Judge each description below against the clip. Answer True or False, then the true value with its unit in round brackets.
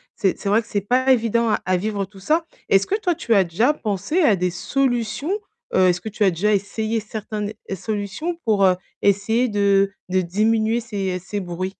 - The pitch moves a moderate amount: True (3.0 semitones)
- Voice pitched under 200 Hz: False (210 Hz)